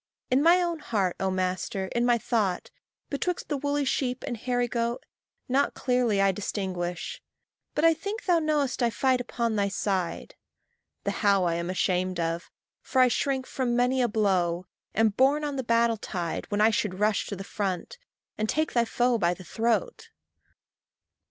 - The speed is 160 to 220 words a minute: Yes, average, 180 wpm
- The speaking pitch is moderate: No, high, 230 Hz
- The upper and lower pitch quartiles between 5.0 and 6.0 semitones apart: Yes, wide, 5.4 semitones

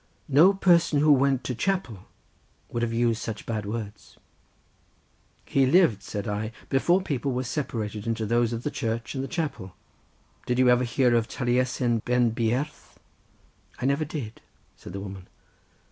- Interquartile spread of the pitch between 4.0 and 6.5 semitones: No, average, 3.6 semitones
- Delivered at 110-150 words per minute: No, average, 160 wpm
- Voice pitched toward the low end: Yes, low, 120 Hz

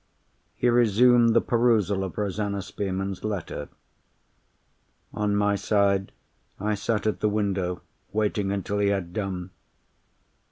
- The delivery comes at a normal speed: No, slow, 120 wpm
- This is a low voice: Yes, low, 100 Hz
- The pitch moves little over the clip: Yes, narrow, 1.7 semitones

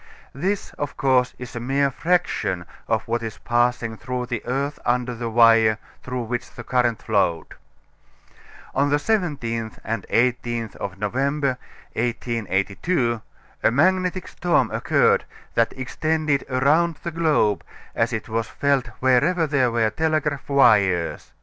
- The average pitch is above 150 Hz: No, low, 125 Hz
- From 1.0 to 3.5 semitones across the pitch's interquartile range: No, average, 3.9 semitones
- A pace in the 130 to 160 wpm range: Yes, slow, 135 wpm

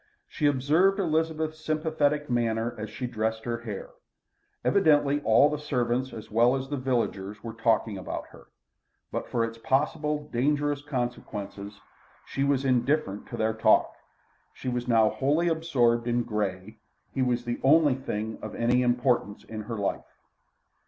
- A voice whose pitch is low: Yes, low, 125 Hz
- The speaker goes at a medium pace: Yes, average, 150 wpm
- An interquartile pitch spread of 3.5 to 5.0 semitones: Yes, average, 4.5 semitones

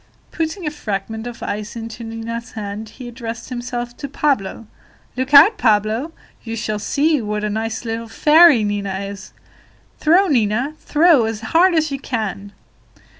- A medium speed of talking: Yes, average, 155 wpm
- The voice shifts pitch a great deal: No, average, 4.8 semitones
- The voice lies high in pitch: Yes, high, 230 Hz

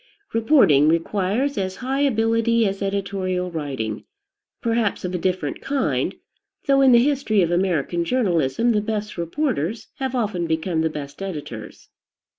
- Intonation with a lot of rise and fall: Yes, wide, 5.8 semitones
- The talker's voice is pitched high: Yes, high, 195 Hz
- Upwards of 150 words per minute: No, average, 140 wpm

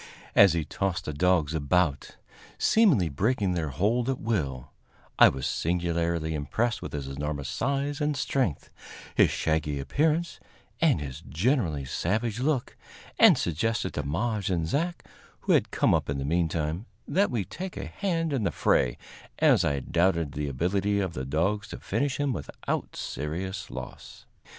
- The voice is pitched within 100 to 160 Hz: No, very low, 90 Hz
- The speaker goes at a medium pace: Yes, average, 160 wpm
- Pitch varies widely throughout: Yes, wide, 8.0 semitones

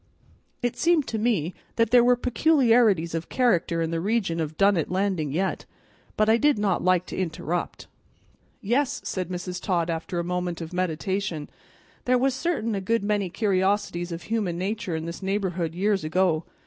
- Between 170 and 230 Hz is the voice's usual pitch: Yes, high, 190 Hz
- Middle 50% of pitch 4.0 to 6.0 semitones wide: Yes, average, 4.7 semitones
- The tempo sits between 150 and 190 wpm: Yes, average, 175 wpm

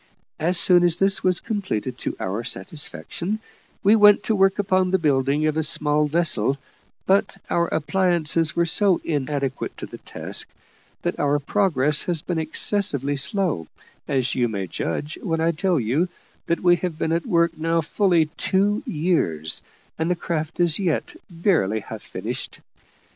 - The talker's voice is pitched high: No, medium, 165 Hz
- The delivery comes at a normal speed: Yes, average, 160 wpm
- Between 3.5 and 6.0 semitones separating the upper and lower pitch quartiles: Yes, average, 4.2 semitones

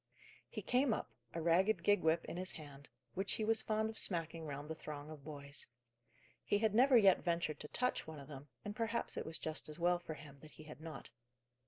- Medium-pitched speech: Yes, medium, 165 Hz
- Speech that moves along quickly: Yes, fast, 225 wpm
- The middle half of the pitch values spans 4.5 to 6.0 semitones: Yes, average, 5.3 semitones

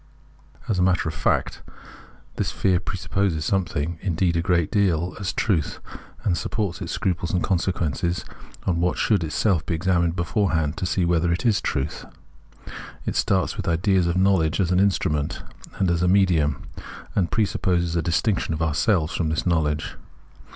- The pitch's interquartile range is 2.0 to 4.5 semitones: Yes, narrow, 2.6 semitones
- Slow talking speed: No, average, 170 wpm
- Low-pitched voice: Yes, very low, 85 Hz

